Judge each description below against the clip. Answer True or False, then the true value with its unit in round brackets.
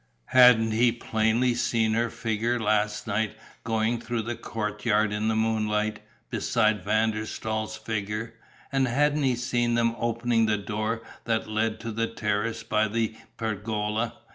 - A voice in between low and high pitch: False (110 Hz)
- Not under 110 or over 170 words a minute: True (150 wpm)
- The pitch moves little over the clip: True (1.4 semitones)